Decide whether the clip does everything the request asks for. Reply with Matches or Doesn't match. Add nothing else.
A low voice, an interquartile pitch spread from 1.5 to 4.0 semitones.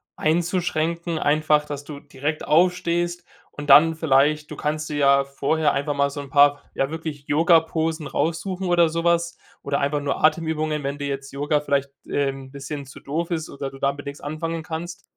Doesn't match